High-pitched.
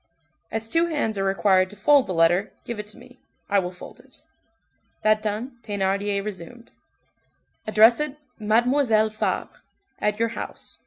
Yes: high, 215 Hz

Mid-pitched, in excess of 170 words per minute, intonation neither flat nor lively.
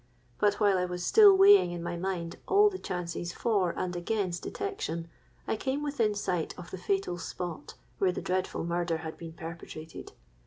Yes: medium, 180 Hz; average, 180 wpm; average, 3.6 semitones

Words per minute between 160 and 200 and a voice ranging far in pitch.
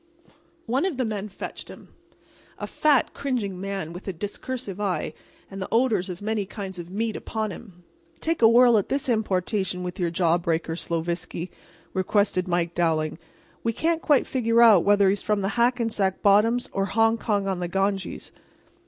No: average, 170 wpm; average, 4.0 semitones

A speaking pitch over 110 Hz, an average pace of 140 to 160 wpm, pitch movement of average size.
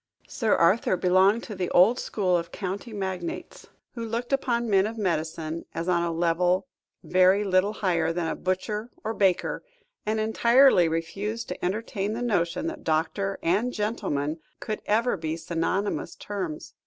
Yes: high, 190 Hz; average, 155 wpm; average, 4.2 semitones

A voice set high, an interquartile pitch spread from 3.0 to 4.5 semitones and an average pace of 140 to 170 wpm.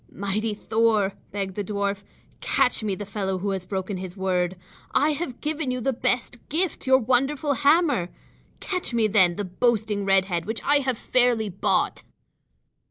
No: high, 215 Hz; average, 5.0 semitones; average, 165 wpm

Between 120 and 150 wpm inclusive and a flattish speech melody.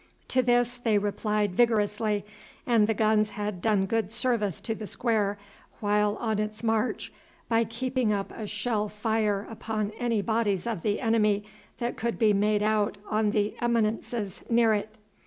No: average, 160 wpm; narrow, 1.7 semitones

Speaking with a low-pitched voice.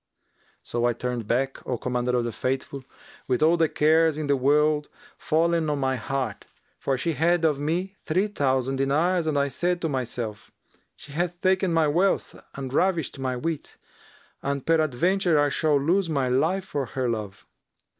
No: medium, 145 Hz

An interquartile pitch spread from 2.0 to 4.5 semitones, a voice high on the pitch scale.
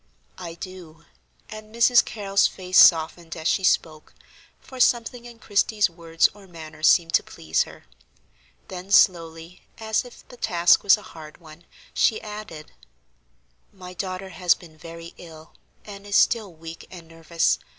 No: average, 3.8 semitones; medium, 180 Hz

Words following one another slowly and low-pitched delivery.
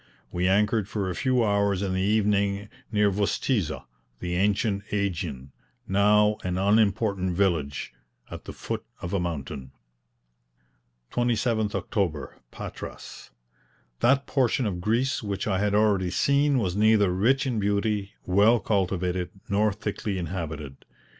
Yes: slow, 130 wpm; low, 100 Hz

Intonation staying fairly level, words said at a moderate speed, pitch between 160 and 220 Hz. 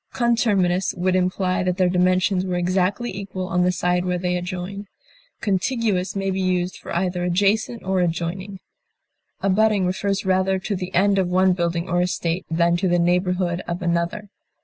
Yes: narrow, 1.4 semitones; average, 170 wpm; medium, 185 Hz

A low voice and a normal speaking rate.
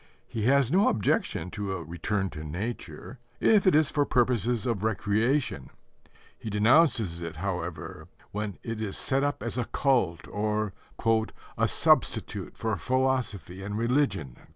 Yes: low, 110 Hz; average, 145 wpm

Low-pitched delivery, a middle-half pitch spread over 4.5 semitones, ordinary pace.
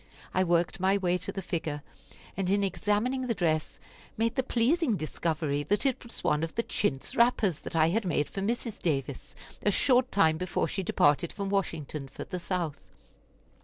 No: medium, 185 Hz; average, 5.1 semitones; average, 185 wpm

